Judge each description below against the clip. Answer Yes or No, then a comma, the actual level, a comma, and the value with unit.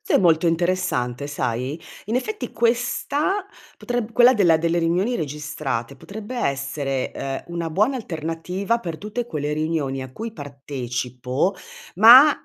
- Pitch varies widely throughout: Yes, wide, 7.9 semitones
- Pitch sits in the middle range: Yes, medium, 165 Hz